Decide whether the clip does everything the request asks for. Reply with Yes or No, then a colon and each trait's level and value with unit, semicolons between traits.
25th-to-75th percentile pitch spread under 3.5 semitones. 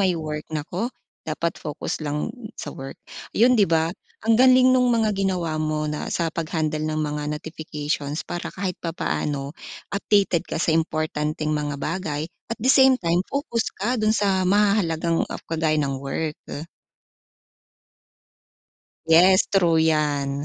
No: average, 4.4 semitones